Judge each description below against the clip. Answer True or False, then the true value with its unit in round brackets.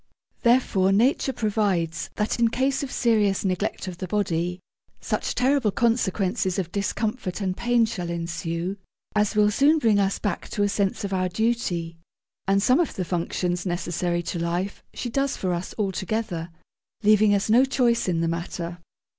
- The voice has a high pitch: True (200 Hz)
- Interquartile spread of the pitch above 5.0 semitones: False (4.4 semitones)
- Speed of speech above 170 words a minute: False (165 wpm)